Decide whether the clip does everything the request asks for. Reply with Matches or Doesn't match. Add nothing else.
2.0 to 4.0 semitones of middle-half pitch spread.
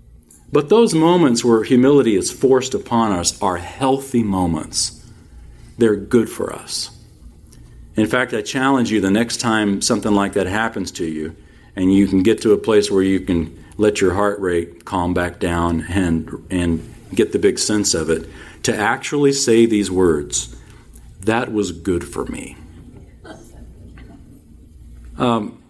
Doesn't match